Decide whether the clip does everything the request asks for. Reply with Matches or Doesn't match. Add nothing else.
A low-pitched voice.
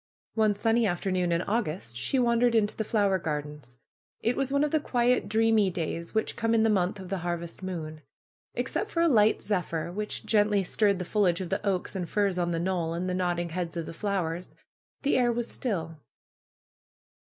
Doesn't match